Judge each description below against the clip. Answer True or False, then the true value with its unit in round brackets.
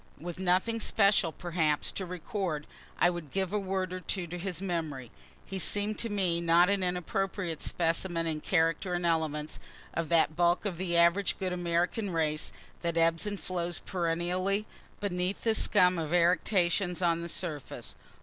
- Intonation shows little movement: True (2.2 semitones)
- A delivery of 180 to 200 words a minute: False (165 wpm)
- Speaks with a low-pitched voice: False (175 Hz)